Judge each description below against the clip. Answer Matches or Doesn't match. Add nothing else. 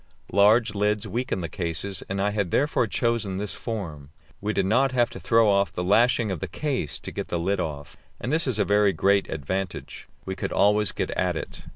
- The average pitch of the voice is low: Matches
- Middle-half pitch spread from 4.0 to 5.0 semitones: Doesn't match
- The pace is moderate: Doesn't match